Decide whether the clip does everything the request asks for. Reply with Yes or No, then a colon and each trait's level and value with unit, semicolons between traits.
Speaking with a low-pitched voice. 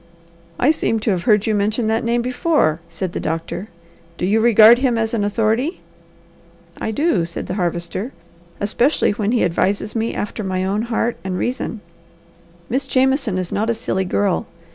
No: high, 220 Hz